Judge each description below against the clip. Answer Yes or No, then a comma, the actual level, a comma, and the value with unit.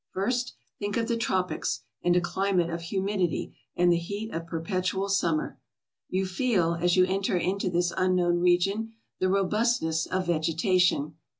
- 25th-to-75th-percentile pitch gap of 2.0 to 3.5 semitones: Yes, narrow, 2.5 semitones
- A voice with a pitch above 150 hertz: Yes, medium, 185 Hz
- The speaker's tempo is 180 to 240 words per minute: No, average, 155 wpm